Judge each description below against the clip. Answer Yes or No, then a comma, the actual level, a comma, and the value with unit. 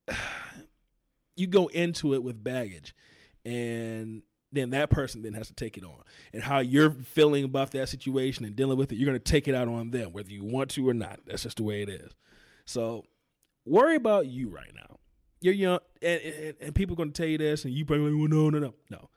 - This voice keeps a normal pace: No, fast, 230 wpm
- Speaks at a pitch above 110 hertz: Yes, low, 135 Hz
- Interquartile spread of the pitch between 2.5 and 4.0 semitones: No, average, 4.7 semitones